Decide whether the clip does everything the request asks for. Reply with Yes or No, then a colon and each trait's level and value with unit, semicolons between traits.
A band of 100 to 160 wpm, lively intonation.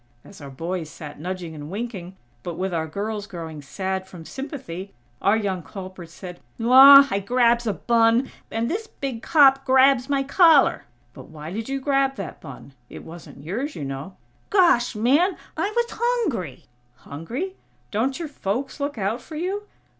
No: average, 170 wpm; wide, 7.5 semitones